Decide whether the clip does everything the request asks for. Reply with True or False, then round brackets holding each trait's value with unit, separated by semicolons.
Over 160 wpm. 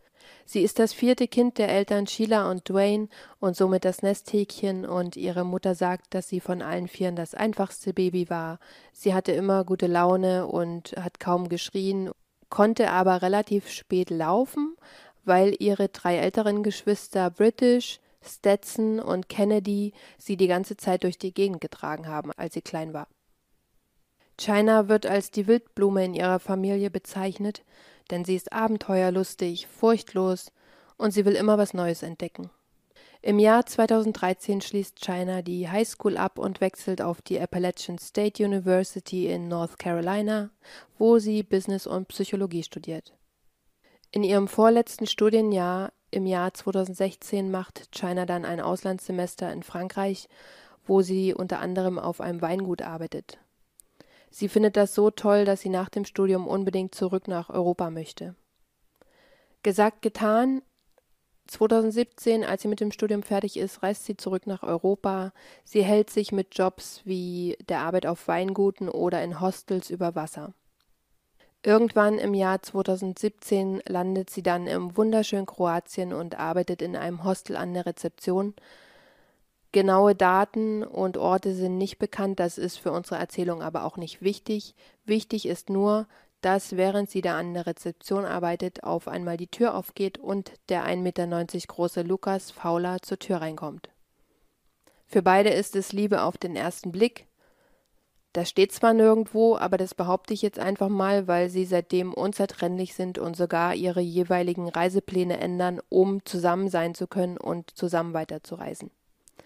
False (150 wpm)